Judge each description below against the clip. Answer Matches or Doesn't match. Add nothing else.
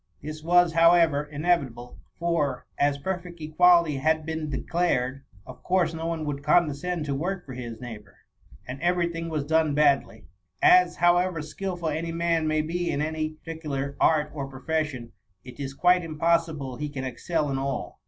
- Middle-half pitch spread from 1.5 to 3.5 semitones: Matches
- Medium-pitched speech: Matches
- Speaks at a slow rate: Doesn't match